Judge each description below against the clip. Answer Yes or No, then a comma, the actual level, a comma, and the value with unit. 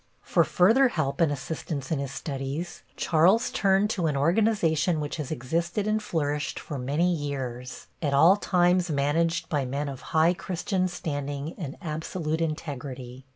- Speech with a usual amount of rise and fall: Yes, average, 3.9 semitones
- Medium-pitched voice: Yes, medium, 155 Hz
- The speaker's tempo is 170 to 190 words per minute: No, average, 155 wpm